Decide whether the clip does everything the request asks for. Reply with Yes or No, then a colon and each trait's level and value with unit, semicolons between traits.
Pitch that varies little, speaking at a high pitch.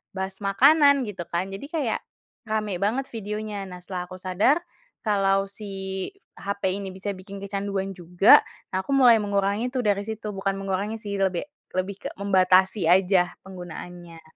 Yes: narrow, 2.0 semitones; high, 195 Hz